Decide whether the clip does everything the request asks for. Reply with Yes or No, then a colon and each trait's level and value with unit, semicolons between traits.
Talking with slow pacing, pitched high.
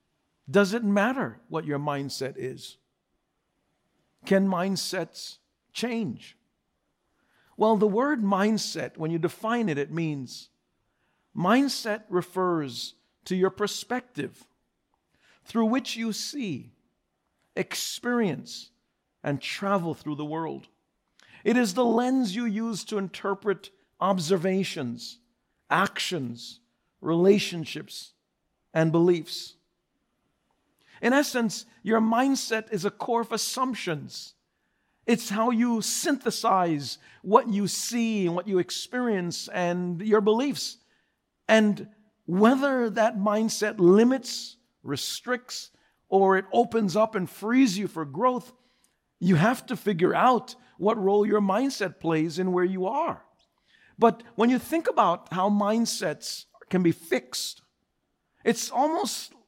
Yes: slow, 115 wpm; high, 205 Hz